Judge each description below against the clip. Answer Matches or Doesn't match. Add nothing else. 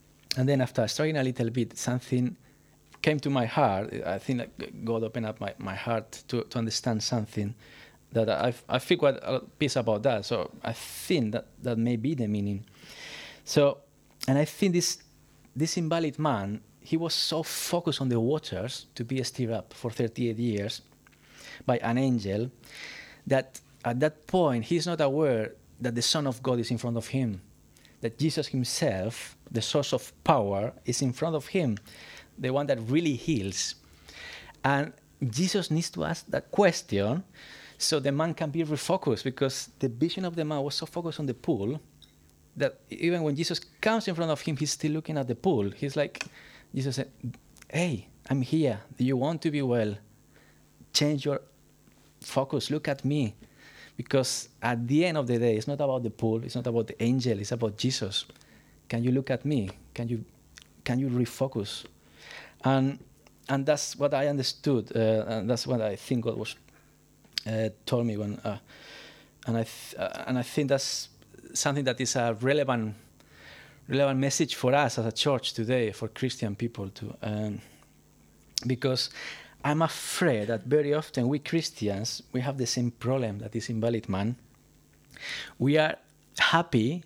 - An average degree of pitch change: Matches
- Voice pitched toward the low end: Matches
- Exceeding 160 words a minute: Matches